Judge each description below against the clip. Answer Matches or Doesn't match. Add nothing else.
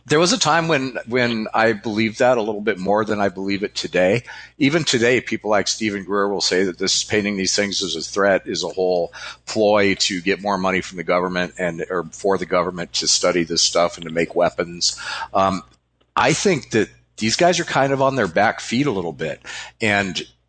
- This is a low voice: Matches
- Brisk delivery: Matches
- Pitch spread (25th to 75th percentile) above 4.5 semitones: Doesn't match